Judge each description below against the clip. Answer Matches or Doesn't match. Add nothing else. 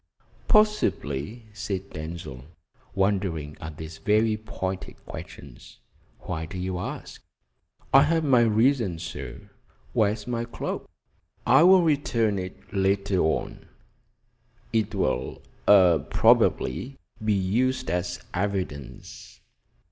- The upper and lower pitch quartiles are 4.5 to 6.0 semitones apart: Matches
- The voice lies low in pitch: Matches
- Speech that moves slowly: Matches